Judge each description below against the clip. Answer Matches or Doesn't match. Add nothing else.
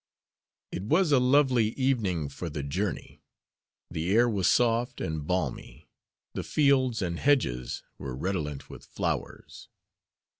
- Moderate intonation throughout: Doesn't match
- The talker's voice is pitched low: Matches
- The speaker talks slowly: Matches